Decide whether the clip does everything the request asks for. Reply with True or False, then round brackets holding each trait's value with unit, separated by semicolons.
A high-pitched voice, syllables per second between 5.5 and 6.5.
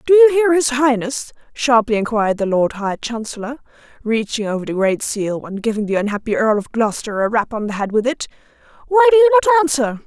True (245 Hz; 6.0 syllables/s)